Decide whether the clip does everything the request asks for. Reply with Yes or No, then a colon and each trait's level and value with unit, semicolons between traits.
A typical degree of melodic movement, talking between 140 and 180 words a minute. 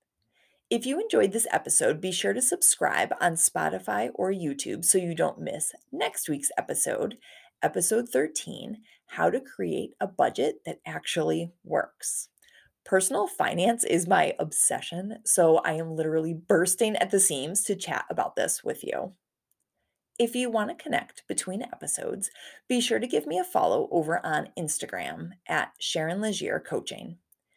No: wide, 5.9 semitones; average, 150 wpm